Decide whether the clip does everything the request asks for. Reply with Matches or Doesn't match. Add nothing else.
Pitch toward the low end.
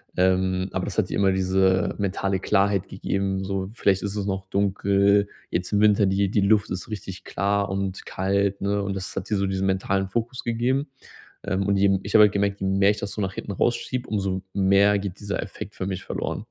Matches